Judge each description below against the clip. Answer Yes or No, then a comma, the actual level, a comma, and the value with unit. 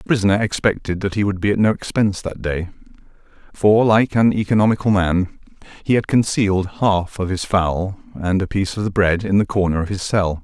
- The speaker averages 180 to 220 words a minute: Yes, fast, 205 wpm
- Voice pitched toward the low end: Yes, low, 100 Hz